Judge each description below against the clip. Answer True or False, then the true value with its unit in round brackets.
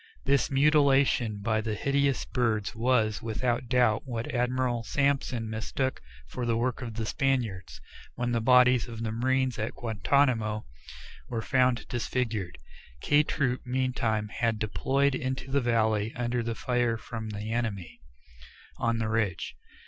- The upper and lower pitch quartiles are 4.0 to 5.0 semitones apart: False (2.6 semitones)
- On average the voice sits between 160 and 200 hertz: False (120 Hz)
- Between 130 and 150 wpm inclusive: True (140 wpm)